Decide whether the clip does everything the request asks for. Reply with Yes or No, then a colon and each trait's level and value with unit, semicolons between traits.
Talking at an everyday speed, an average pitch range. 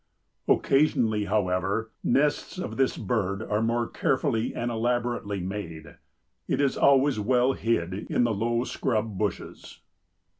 No: slow, 125 wpm; average, 3.3 semitones